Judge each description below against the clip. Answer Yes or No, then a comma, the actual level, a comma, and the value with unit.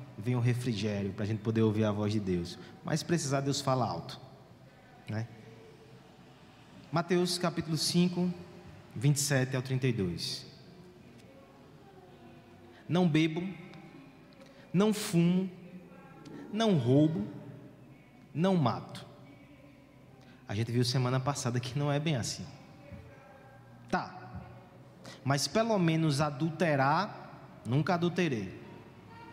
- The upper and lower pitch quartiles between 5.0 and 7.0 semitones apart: Yes, wide, 5.4 semitones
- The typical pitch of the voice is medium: Yes, medium, 145 Hz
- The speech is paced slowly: Yes, slow, 100 wpm